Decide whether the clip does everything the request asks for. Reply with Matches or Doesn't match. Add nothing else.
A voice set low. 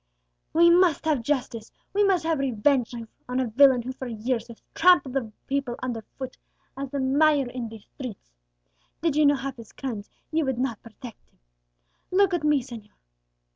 Doesn't match